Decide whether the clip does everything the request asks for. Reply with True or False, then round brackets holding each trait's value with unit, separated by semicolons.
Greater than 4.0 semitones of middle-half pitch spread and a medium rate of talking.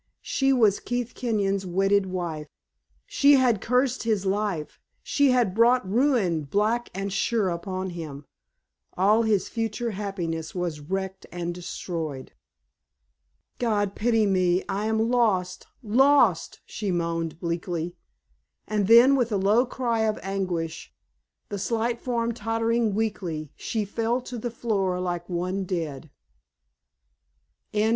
False (4.5 semitones; 125 wpm)